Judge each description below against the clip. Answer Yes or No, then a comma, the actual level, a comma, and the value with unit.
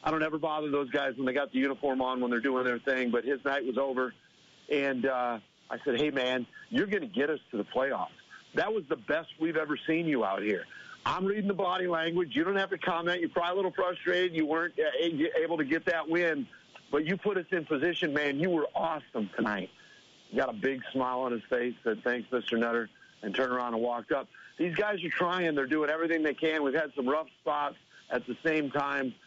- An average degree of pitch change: Yes, average, 4.6 semitones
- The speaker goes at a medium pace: No, fast, 235 wpm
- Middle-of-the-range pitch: Yes, medium, 150 Hz